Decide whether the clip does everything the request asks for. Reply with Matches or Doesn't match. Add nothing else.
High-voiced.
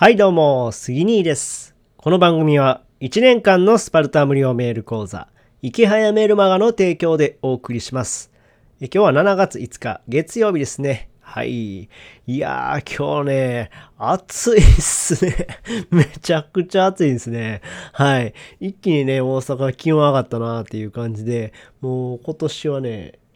Doesn't match